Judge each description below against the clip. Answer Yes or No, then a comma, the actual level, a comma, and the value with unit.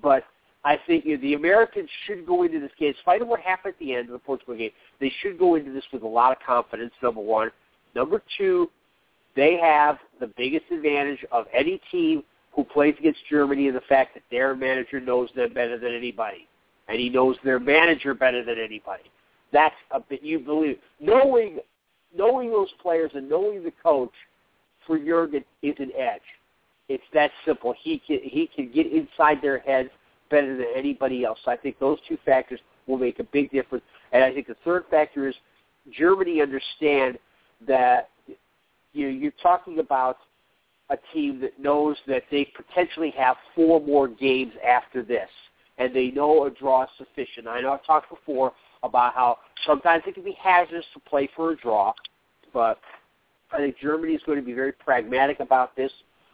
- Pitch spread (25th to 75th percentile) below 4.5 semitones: No, average, 4.9 semitones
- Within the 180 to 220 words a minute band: Yes, average, 185 wpm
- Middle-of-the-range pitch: Yes, medium, 145 Hz